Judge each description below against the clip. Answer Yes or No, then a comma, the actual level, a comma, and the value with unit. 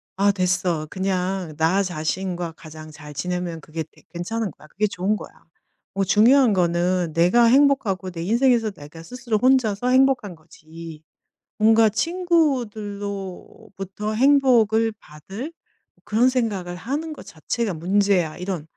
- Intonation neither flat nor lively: Yes, average, 4.8 semitones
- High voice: Yes, high, 195 Hz